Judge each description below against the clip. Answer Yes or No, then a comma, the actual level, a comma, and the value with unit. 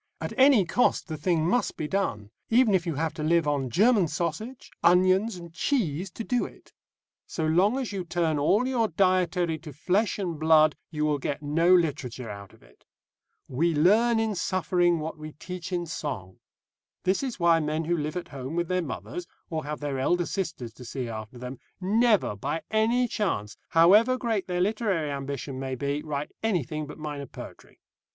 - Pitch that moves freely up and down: No, average, 4.7 semitones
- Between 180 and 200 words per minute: Yes, average, 190 wpm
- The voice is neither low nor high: Yes, medium, 165 Hz